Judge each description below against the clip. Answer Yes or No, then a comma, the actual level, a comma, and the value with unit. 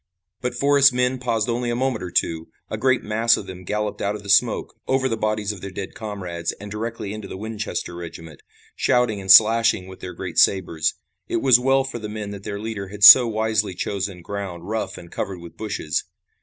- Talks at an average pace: No, fast, 210 wpm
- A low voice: Yes, low, 105 Hz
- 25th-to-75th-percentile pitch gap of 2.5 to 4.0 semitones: Yes, average, 3.4 semitones